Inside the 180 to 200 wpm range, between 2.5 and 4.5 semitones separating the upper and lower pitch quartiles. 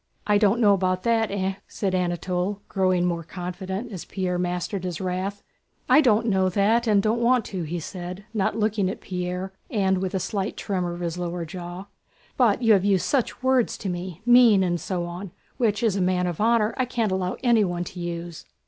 Yes: average, 195 wpm; average, 3.1 semitones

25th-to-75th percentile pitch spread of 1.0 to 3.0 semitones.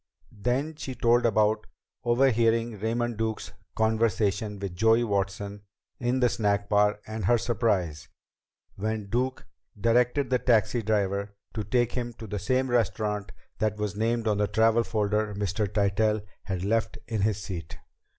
Yes: narrow, 2.4 semitones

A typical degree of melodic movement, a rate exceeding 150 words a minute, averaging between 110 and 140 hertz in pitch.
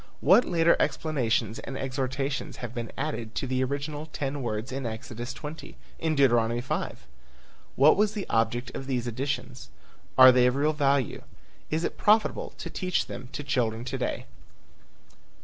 Yes: average, 3.5 semitones; average, 160 wpm; low, 135 Hz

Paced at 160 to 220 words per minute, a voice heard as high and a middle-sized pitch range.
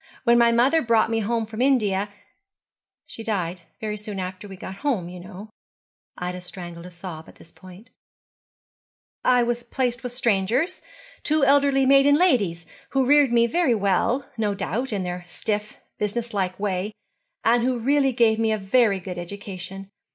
Yes: average, 165 wpm; high, 220 Hz; average, 4.6 semitones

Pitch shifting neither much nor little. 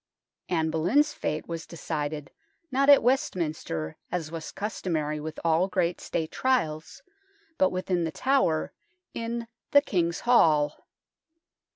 No: wide, 6.7 semitones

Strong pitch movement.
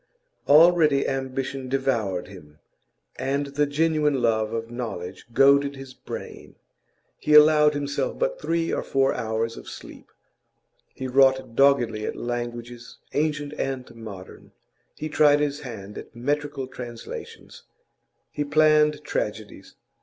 No: average, 3.9 semitones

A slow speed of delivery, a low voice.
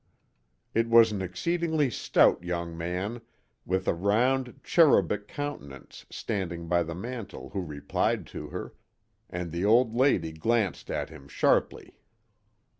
Yes: slow, 130 wpm; low, 100 Hz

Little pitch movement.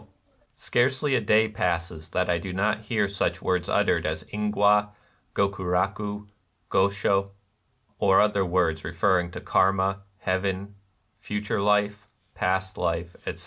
Yes: narrow, 2.1 semitones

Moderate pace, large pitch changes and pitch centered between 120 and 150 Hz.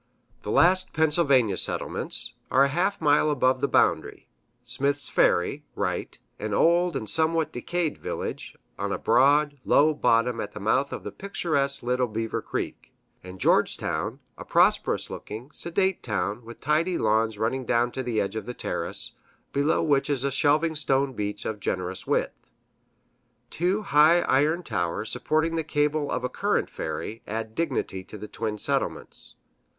Yes: average, 160 wpm; wide, 5.8 semitones; low, 135 Hz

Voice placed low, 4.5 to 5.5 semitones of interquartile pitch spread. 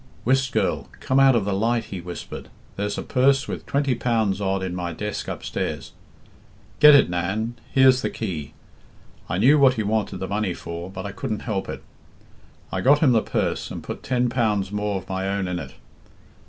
Yes: low, 105 Hz; average, 4.9 semitones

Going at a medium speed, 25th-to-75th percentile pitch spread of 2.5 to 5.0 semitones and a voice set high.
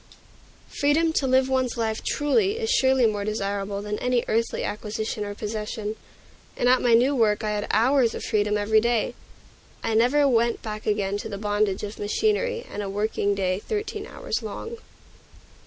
Yes: average, 170 wpm; average, 4.1 semitones; high, 220 Hz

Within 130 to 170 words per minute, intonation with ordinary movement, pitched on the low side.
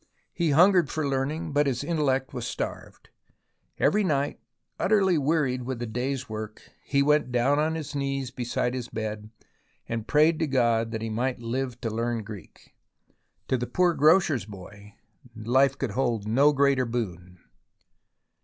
Yes: average, 155 wpm; average, 4.3 semitones; low, 130 Hz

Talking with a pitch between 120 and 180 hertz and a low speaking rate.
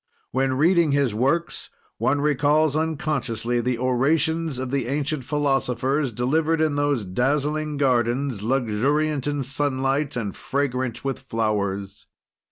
Yes: low, 135 Hz; slow, 120 wpm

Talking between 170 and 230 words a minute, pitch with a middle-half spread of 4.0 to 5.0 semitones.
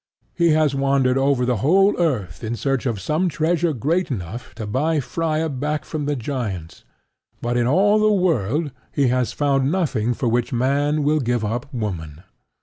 Yes: average, 175 wpm; average, 4.5 semitones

